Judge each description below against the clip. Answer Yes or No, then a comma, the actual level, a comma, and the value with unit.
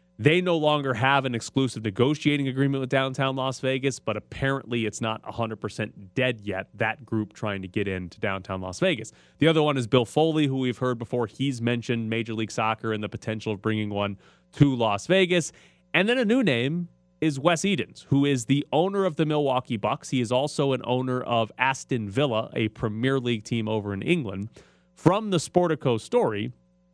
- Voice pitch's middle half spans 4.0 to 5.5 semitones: Yes, average, 4.8 semitones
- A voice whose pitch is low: Yes, low, 125 Hz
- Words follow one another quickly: No, average, 195 wpm